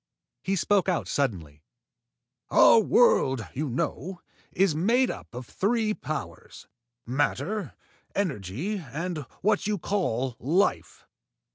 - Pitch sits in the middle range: Yes, medium, 170 Hz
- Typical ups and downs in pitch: No, wide, 7.6 semitones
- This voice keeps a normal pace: No, slow, 110 wpm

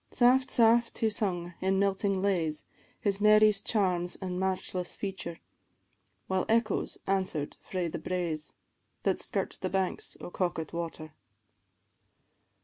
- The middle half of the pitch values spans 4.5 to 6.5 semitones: No, average, 2.8 semitones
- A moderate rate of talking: No, slow, 125 wpm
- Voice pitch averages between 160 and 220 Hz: Yes, high, 190 Hz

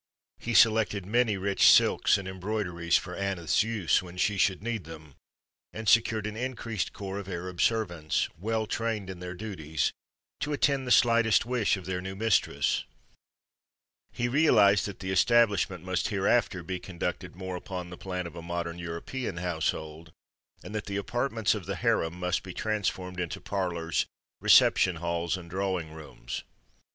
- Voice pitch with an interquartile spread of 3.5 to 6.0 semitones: Yes, average, 3.9 semitones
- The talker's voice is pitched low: Yes, very low, 95 Hz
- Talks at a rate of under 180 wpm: Yes, average, 160 wpm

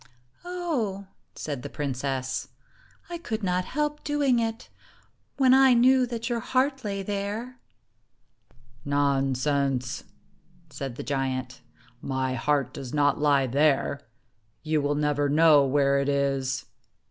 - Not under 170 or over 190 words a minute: No, slow, 135 wpm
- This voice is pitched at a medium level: Yes, medium, 145 Hz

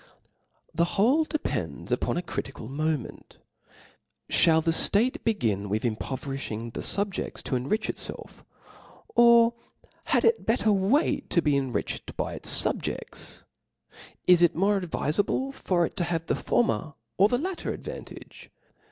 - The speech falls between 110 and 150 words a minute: Yes, average, 145 wpm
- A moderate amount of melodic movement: No, wide, 8.3 semitones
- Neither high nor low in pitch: Yes, medium, 175 Hz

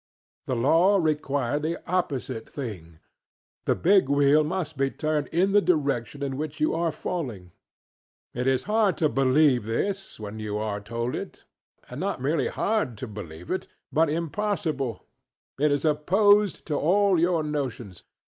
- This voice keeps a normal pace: Yes, average, 150 wpm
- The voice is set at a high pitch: No, medium, 145 Hz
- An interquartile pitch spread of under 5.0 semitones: No, wide, 5.5 semitones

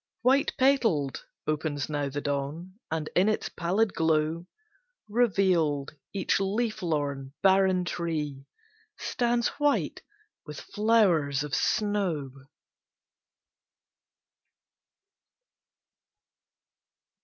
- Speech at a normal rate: No, slow, 80 wpm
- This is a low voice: No, medium, 170 Hz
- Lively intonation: Yes, wide, 5.9 semitones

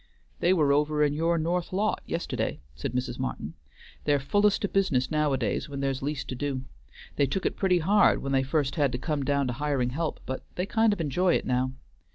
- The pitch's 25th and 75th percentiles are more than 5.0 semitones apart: No, average, 4.3 semitones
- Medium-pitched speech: Yes, medium, 145 Hz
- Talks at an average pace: No, fast, 210 wpm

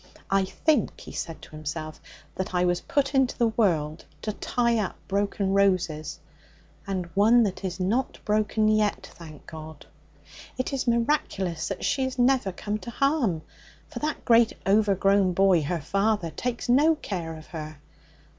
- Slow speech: No, average, 160 wpm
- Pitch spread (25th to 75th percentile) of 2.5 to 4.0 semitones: No, average, 5.3 semitones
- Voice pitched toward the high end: Yes, high, 200 Hz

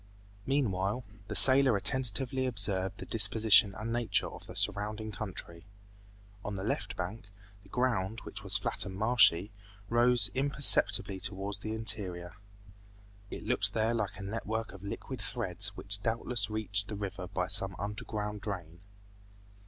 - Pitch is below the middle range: Yes, low, 105 Hz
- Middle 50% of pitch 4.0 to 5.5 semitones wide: No, narrow, 2.6 semitones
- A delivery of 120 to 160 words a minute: Yes, average, 145 wpm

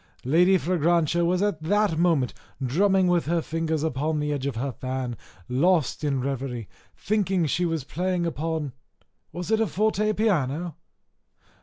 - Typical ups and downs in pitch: Yes, average, 4.5 semitones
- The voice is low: No, medium, 165 Hz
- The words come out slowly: No, average, 155 wpm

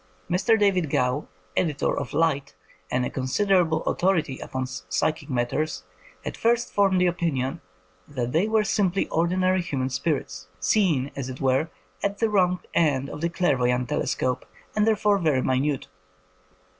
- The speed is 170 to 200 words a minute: No, average, 150 wpm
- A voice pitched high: No, medium, 155 Hz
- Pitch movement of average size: No, wide, 6.1 semitones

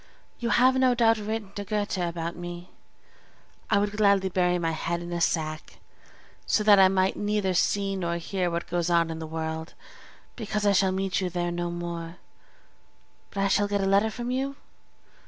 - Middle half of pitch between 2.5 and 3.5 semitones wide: Yes, average, 3.2 semitones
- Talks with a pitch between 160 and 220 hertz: Yes, high, 190 Hz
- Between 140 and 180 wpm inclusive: No, average, 190 wpm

